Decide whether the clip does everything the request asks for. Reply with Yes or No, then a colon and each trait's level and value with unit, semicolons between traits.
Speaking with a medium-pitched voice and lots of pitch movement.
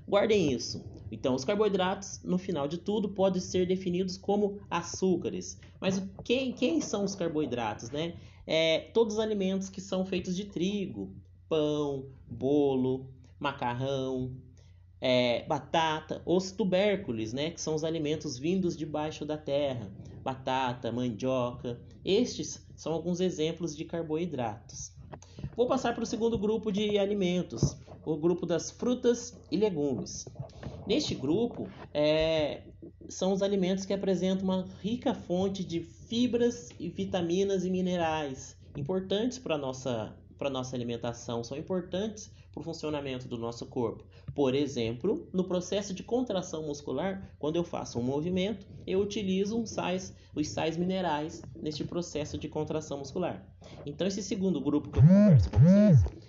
Yes: medium, 160 Hz; wide, 6.1 semitones